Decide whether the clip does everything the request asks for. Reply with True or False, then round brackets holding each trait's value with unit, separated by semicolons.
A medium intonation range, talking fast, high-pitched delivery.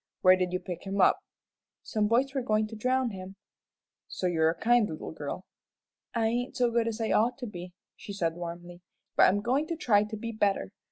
True (4.5 semitones; 215 wpm; 210 Hz)